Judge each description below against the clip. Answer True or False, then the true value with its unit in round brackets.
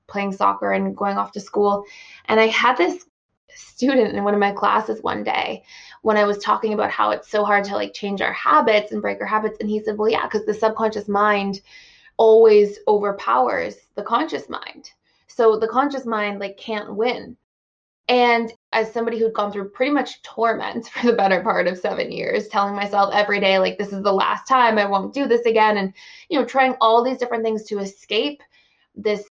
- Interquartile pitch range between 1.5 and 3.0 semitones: True (2.6 semitones)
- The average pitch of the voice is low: False (215 Hz)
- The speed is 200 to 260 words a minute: True (205 wpm)